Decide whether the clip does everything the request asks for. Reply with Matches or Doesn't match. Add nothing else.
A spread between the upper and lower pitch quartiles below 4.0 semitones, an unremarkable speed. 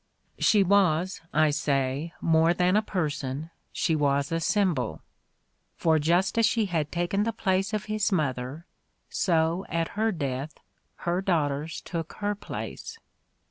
Doesn't match